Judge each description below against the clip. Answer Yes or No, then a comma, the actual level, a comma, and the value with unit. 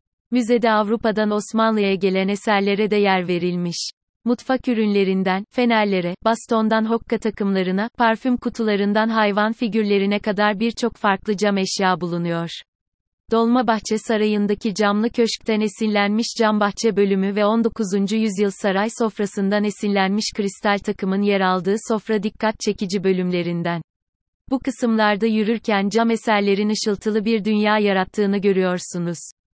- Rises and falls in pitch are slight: Yes, narrow, 2.1 semitones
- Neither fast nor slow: Yes, average, 115 wpm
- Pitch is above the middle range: Yes, high, 210 Hz